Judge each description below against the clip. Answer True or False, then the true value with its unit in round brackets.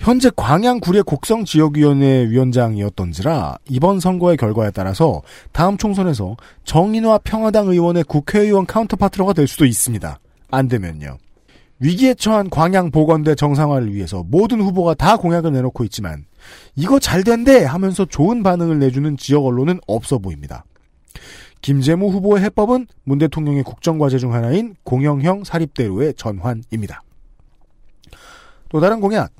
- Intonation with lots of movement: True (7.8 semitones)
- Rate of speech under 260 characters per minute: False (345 characters per minute)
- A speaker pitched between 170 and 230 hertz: False (155 Hz)